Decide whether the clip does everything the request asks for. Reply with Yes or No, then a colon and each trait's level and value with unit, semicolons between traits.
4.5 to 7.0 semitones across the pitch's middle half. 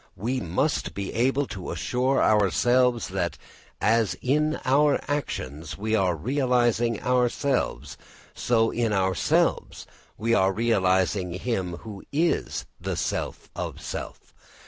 Yes: average, 5.1 semitones